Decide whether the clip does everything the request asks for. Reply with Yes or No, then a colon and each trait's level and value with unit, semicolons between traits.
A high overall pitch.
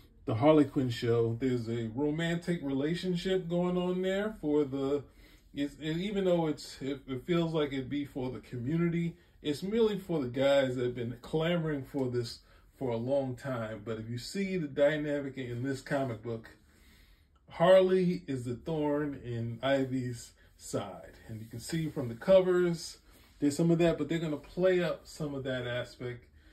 No: medium, 140 Hz